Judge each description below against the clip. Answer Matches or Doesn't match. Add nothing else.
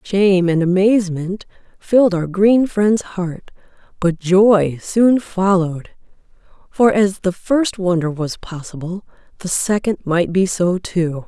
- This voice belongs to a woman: Matches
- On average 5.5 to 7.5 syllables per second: Doesn't match